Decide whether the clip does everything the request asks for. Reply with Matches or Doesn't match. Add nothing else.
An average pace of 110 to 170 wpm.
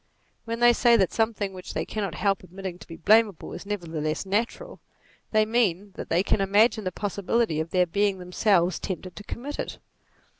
Doesn't match